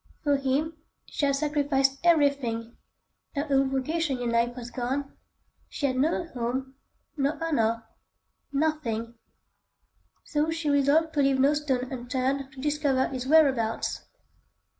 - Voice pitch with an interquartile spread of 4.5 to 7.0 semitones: No, narrow, 2.6 semitones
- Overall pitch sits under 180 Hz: No, very high, 275 Hz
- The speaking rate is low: Yes, slow, 125 wpm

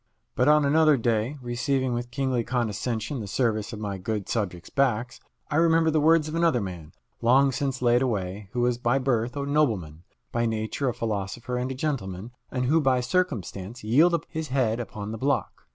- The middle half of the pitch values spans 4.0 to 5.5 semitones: Yes, average, 4.3 semitones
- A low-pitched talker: Yes, low, 125 Hz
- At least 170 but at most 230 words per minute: Yes, average, 190 wpm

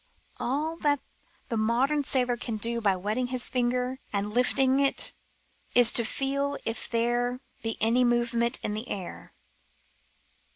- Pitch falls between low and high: No, high, 245 Hz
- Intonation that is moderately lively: No, narrow, 2.3 semitones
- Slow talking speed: No, average, 150 wpm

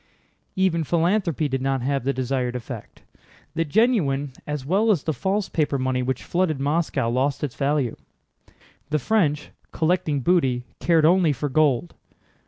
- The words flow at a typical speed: Yes, average, 150 wpm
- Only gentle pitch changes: No, average, 4.4 semitones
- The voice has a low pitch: No, medium, 150 Hz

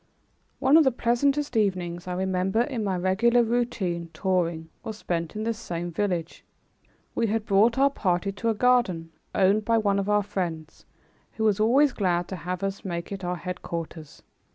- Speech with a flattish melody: No, average, 4.5 semitones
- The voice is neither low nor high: No, high, 195 Hz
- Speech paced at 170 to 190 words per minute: Yes, average, 175 wpm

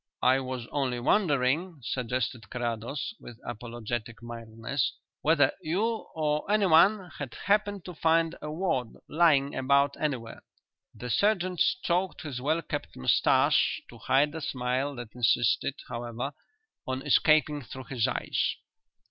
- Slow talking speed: Yes, slow, 130 wpm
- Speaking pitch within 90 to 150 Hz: Yes, medium, 140 Hz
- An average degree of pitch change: Yes, average, 5.0 semitones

